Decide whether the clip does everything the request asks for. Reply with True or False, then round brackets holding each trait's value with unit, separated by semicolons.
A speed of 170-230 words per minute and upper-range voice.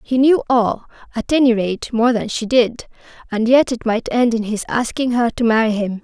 True (200 wpm; 235 Hz)